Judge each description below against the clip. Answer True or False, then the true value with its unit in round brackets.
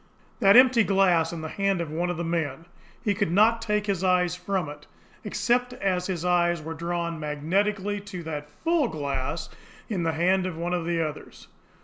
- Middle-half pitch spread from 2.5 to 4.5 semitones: True (3.4 semitones)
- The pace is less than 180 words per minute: False (195 wpm)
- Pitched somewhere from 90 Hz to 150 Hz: False (175 Hz)